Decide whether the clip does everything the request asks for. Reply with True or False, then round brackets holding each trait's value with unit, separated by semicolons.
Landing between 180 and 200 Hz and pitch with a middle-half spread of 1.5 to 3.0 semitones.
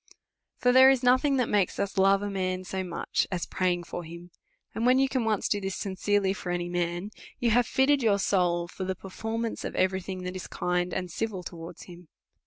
False (190 Hz; 3.9 semitones)